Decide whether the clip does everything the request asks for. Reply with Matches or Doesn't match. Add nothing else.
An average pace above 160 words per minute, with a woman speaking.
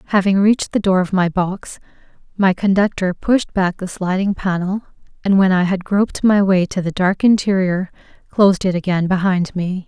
Matches